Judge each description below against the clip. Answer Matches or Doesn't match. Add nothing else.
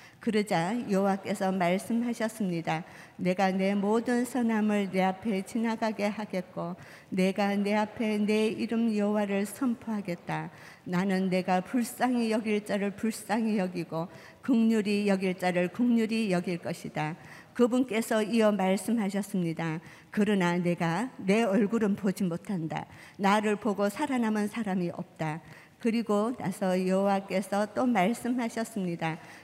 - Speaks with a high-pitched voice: Matches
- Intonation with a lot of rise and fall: Doesn't match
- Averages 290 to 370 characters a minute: Doesn't match